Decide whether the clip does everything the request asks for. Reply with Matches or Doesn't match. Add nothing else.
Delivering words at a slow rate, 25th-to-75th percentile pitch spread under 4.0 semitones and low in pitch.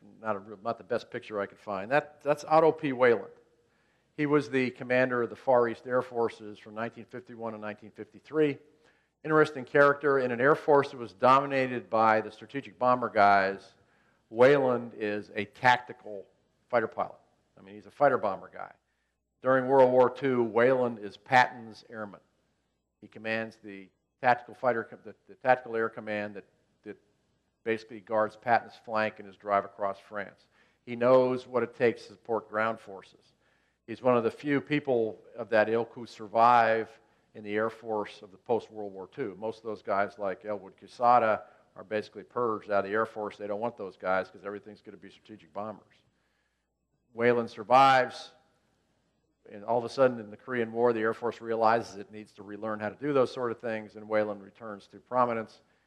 Doesn't match